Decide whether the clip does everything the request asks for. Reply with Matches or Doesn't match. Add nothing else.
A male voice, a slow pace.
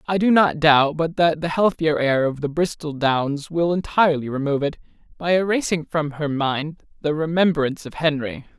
Doesn't match